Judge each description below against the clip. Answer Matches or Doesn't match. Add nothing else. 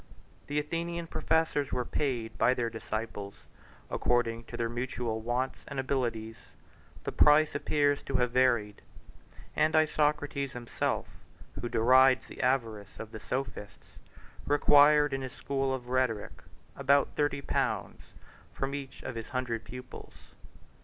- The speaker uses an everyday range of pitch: Matches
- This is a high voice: Doesn't match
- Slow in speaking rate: Matches